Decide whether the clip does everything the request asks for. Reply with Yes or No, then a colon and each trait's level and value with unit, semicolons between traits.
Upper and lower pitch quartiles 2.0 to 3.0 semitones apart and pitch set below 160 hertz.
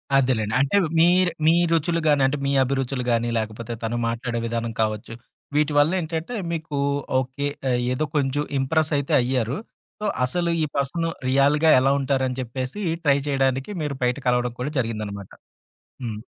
No: average, 3.5 semitones; low, 135 Hz